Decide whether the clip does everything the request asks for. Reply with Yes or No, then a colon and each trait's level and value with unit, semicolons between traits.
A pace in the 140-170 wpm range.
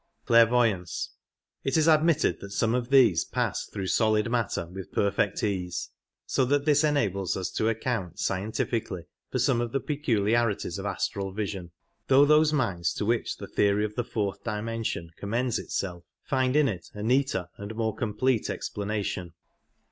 Yes: average, 165 wpm